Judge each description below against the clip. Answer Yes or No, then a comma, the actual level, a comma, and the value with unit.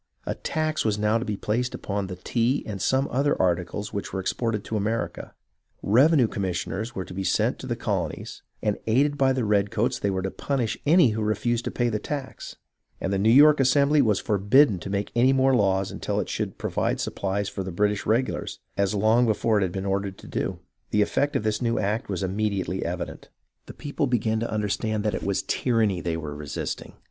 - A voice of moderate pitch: No, low, 105 Hz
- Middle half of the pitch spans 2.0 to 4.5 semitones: Yes, average, 3.9 semitones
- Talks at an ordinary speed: No, fast, 210 wpm